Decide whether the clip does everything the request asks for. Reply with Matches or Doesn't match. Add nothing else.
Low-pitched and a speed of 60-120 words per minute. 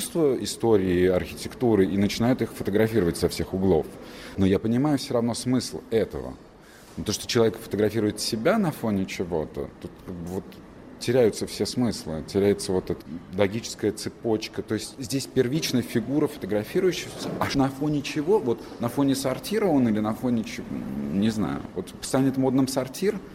Doesn't match